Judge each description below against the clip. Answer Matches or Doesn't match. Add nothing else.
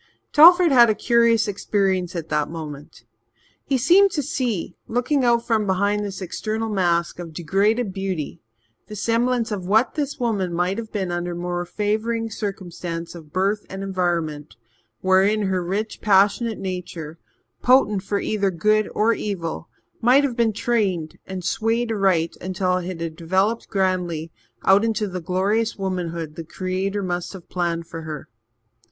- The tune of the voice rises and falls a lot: Doesn't match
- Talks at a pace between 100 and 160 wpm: Matches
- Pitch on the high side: Matches